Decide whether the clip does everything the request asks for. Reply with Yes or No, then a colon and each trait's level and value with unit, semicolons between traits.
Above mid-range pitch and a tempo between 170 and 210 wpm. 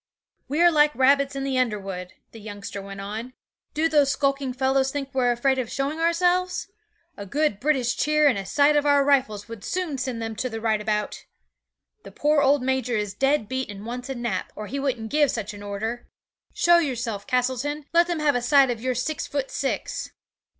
Yes: very high, 260 Hz; average, 200 wpm